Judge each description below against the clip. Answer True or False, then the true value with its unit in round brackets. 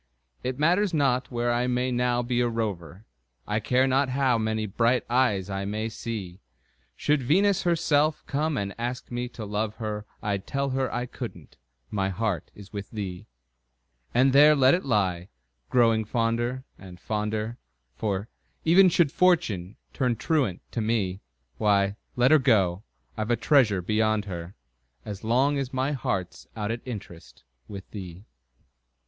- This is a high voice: False (115 Hz)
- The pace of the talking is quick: False (155 wpm)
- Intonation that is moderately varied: True (4.3 semitones)